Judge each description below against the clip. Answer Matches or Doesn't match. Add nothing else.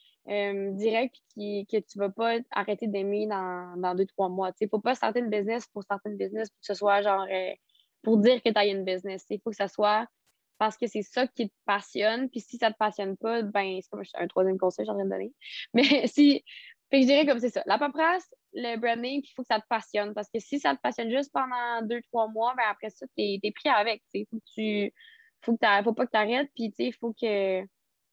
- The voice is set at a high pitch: Matches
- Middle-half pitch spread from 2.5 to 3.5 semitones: Matches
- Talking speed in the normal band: Doesn't match